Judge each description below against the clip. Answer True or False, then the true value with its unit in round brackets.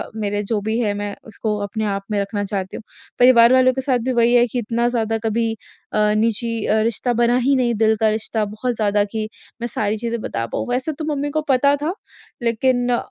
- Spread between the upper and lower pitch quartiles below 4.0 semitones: True (2.5 semitones)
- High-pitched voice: True (230 Hz)